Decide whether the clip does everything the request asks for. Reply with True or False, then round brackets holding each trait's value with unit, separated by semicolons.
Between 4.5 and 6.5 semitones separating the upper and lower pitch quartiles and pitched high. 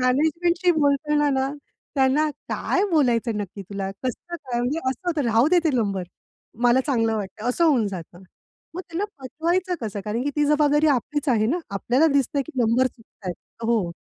True (5.2 semitones; 260 Hz)